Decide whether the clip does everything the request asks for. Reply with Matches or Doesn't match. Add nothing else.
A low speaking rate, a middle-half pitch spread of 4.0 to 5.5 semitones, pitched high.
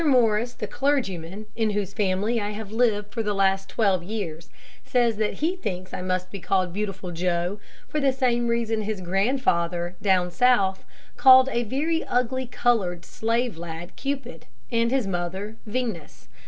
Doesn't match